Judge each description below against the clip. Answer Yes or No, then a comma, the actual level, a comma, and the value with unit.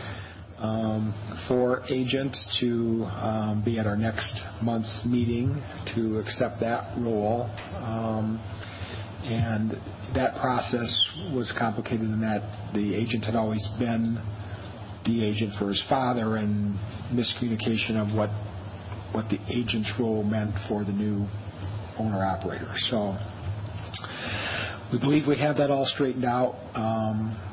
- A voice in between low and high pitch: No, low, 110 Hz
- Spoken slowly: Yes, slow, 120 wpm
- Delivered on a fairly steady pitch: Yes, narrow, 2.1 semitones